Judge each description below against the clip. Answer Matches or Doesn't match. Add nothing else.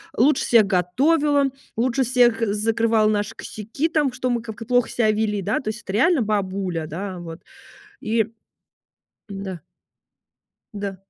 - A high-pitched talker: Matches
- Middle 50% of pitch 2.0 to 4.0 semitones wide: Matches